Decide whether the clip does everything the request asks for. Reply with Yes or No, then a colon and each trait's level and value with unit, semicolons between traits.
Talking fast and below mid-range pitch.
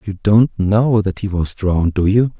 Yes: fast, 225 wpm; low, 100 Hz